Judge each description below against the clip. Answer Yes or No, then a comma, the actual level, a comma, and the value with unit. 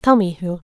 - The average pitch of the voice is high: Yes, high, 195 Hz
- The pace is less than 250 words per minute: No, fast, 255 wpm